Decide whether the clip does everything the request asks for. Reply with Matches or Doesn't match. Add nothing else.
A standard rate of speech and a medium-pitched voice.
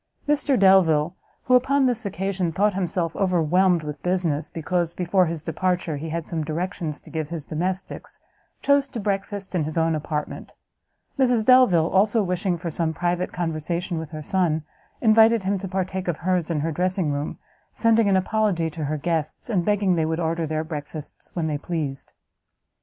Matches